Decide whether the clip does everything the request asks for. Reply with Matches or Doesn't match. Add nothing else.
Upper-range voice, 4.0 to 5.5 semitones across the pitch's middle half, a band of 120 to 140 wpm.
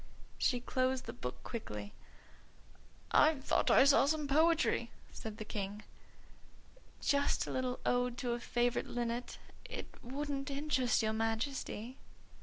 Doesn't match